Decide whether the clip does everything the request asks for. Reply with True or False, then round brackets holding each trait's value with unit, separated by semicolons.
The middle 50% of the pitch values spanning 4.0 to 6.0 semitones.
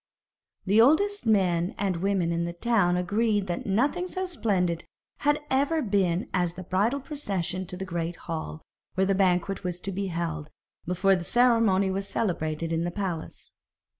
True (4.3 semitones)